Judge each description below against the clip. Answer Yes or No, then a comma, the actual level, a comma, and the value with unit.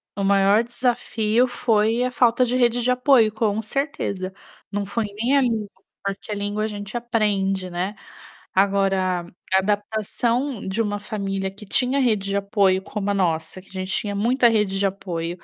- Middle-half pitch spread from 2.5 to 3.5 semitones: Yes, average, 3.2 semitones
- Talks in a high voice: Yes, high, 210 Hz